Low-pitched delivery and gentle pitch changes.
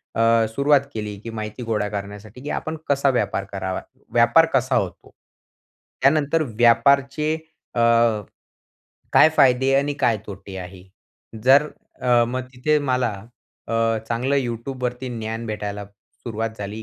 No: low, 120 Hz; average, 4.4 semitones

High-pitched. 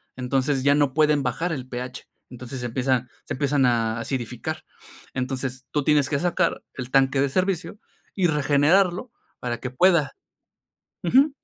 No: low, 135 Hz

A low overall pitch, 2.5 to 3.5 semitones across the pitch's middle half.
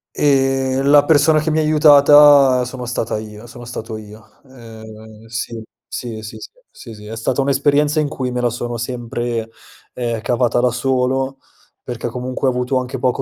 Yes: low, 125 Hz; average, 2.9 semitones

